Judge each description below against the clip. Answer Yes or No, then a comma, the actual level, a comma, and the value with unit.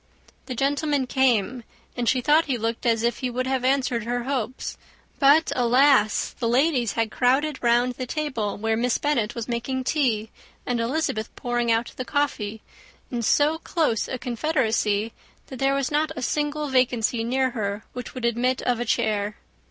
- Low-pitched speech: No, high, 245 Hz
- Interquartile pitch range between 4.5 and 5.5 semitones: No, average, 2.9 semitones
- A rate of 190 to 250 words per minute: No, average, 175 wpm